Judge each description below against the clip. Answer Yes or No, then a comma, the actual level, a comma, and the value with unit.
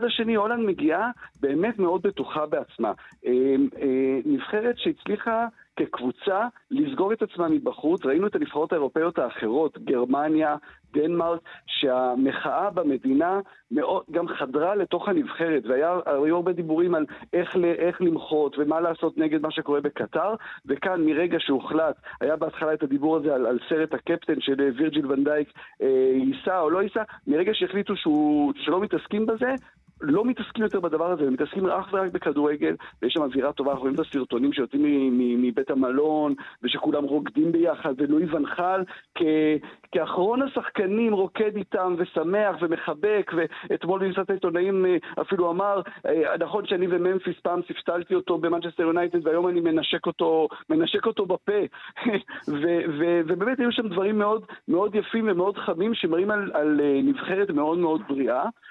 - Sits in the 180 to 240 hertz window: No, medium, 170 Hz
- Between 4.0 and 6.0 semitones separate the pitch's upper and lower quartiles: Yes, average, 5.1 semitones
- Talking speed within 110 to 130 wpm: No, average, 145 wpm